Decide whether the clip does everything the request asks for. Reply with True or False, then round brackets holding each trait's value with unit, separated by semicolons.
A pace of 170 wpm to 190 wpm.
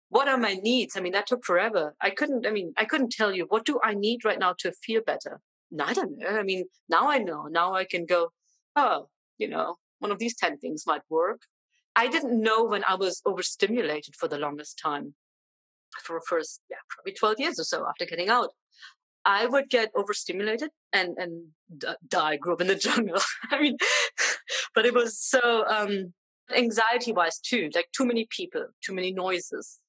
False (200 wpm)